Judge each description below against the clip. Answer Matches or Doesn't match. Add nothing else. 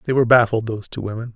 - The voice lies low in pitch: Matches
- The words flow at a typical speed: Doesn't match